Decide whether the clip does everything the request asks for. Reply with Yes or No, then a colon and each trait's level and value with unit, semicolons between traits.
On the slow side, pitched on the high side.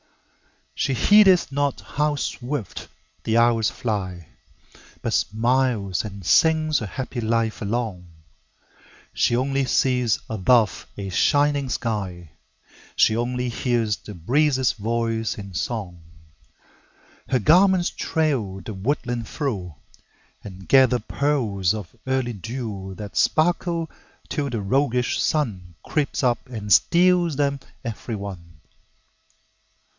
No: slow, 110 wpm; low, 120 Hz